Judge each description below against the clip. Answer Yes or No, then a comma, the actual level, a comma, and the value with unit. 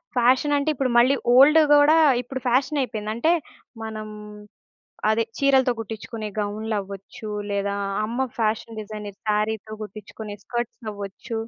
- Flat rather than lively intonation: No, average, 3.6 semitones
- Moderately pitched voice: No, high, 225 Hz